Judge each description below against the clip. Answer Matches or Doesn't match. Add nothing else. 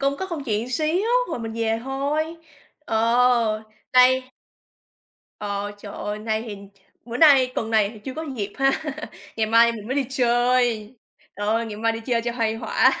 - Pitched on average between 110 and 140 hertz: Doesn't match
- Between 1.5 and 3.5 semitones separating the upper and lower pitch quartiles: Matches